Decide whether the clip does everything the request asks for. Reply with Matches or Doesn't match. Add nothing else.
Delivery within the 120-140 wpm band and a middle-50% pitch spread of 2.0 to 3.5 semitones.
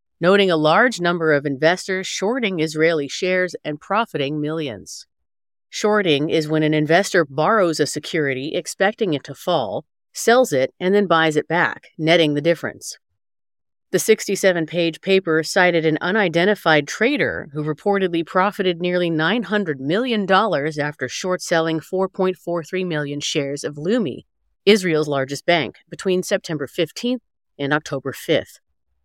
Doesn't match